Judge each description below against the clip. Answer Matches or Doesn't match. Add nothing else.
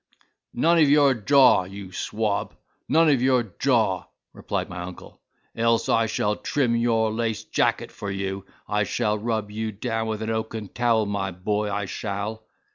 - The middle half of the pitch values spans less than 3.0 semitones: Matches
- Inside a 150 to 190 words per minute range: Matches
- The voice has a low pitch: Matches